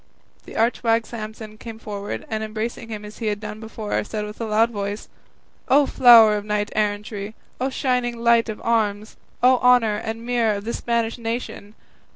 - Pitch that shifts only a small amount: Yes, narrow, 1.8 semitones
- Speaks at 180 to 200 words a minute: Yes, average, 185 wpm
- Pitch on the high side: Yes, high, 220 Hz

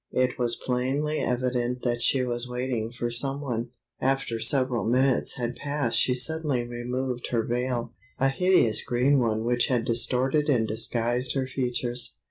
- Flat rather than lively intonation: Yes, narrow, 1.8 semitones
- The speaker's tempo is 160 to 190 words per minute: No, average, 150 wpm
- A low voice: Yes, low, 125 Hz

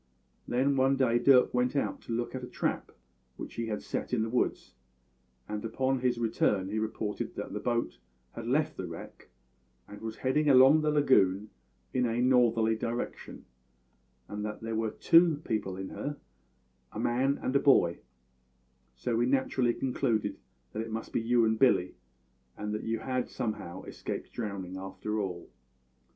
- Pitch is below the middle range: Yes, low, 115 Hz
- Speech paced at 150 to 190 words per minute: Yes, average, 170 wpm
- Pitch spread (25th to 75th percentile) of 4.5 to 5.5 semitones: No, average, 3.3 semitones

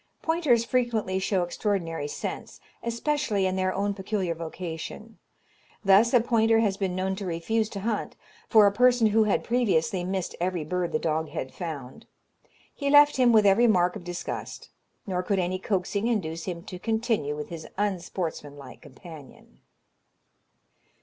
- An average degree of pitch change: Yes, average, 4.5 semitones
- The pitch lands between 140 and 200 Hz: Yes, high, 190 Hz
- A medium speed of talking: Yes, average, 155 wpm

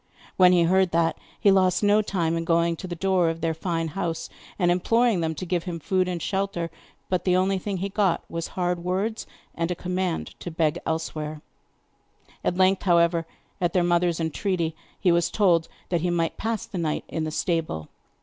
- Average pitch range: No, narrow, 2.1 semitones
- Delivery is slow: No, average, 200 wpm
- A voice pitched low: No, medium, 175 Hz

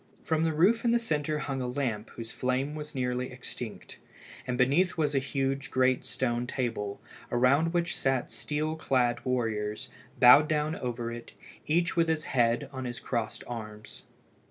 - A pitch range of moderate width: Yes, average, 4.0 semitones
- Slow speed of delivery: No, average, 165 wpm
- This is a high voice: No, low, 130 Hz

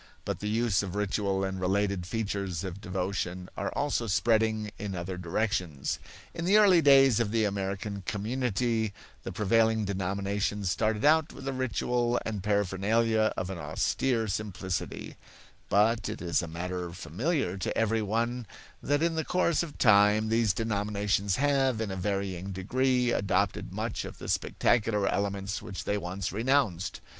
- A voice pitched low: Yes, low, 105 Hz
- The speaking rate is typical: Yes, average, 155 wpm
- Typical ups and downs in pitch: Yes, average, 3.4 semitones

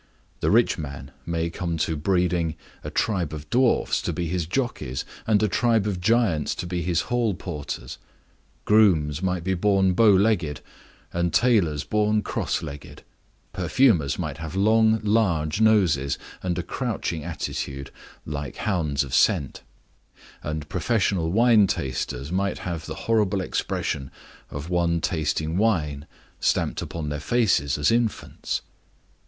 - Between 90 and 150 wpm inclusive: Yes, average, 140 wpm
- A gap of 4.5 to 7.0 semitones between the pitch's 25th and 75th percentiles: Yes, wide, 5.6 semitones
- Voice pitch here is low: Yes, very low, 90 Hz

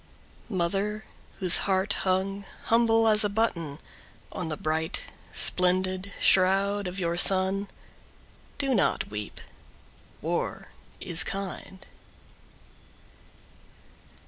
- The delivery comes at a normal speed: No, slow, 90 wpm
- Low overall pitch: No, high, 190 Hz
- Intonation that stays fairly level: Yes, narrow, 2.0 semitones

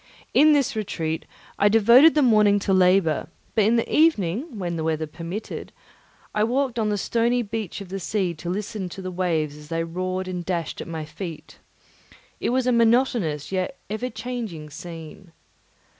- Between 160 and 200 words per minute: Yes, average, 175 wpm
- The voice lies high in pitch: Yes, high, 195 Hz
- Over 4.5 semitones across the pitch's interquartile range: Yes, wide, 5.5 semitones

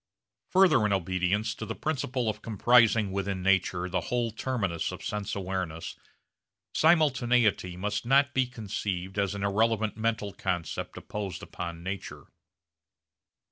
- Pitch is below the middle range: Yes, low, 105 Hz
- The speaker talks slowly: Yes, slow, 130 wpm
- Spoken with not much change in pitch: No, average, 4.0 semitones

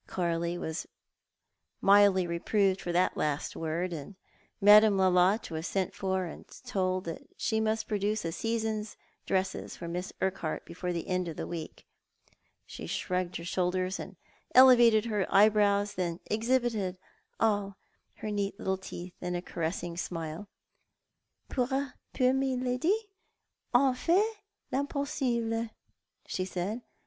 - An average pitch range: Yes, average, 4.0 semitones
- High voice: Yes, high, 195 Hz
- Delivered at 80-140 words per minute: Yes, slow, 135 wpm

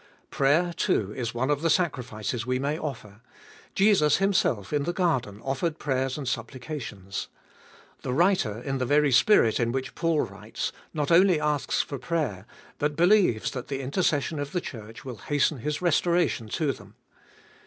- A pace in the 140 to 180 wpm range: Yes, average, 165 wpm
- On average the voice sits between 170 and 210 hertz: No, medium, 140 Hz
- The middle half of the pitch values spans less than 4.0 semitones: No, average, 5.1 semitones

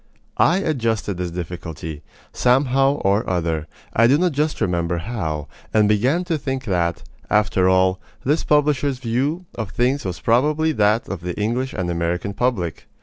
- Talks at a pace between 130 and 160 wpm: Yes, average, 155 wpm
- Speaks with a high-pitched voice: No, low, 110 Hz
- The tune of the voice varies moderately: No, wide, 7.2 semitones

